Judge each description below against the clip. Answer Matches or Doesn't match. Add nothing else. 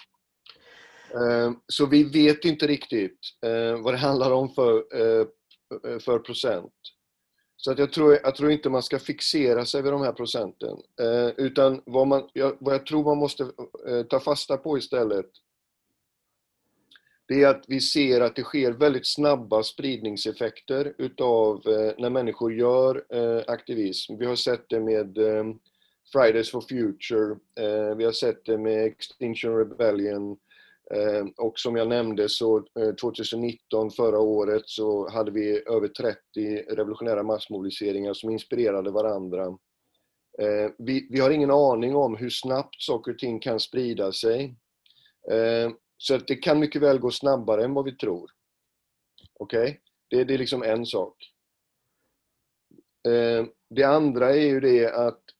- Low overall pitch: Matches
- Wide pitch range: Doesn't match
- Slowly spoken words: Doesn't match